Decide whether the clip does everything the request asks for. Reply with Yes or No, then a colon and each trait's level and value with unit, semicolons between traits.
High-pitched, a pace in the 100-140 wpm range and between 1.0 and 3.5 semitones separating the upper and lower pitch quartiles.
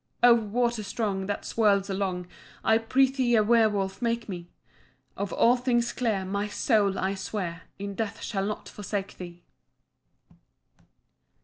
Yes: high, 205 Hz; slow, 135 wpm; average, 3.2 semitones